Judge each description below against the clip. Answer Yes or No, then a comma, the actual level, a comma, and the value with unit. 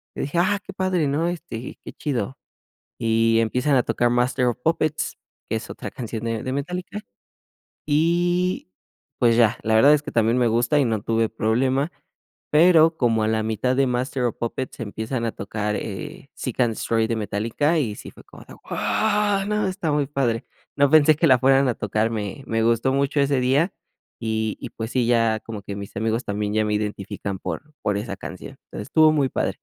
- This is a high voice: No, low, 125 Hz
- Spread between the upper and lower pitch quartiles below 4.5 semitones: No, average, 5.0 semitones